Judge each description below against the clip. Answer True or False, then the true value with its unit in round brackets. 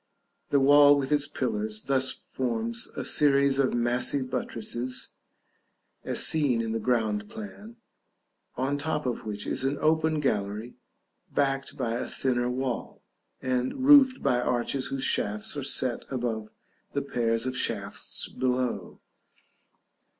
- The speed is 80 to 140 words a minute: True (135 wpm)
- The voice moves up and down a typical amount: True (3.2 semitones)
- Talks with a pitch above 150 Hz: False (130 Hz)